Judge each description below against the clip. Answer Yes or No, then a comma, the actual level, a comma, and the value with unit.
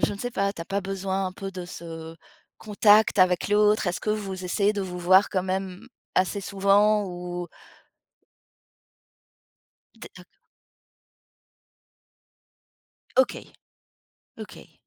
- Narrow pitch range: Yes, narrow, 2.2 semitones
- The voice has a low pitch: No, high, 195 Hz